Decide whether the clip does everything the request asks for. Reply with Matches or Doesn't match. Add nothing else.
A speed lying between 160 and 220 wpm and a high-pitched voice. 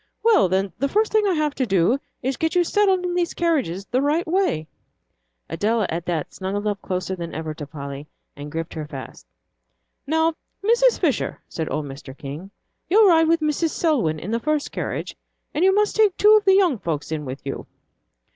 Matches